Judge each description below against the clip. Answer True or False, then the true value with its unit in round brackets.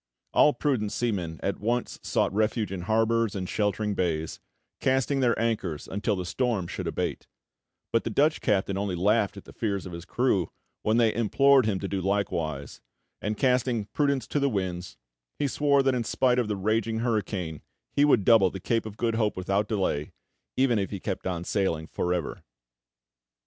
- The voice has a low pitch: True (105 Hz)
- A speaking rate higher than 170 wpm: True (185 wpm)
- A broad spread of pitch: False (4.1 semitones)